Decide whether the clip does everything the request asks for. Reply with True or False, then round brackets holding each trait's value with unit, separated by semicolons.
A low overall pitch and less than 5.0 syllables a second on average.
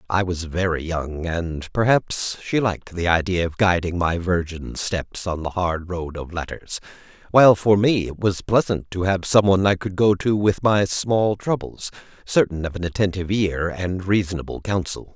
True (95 Hz; 4.7 syllables/s)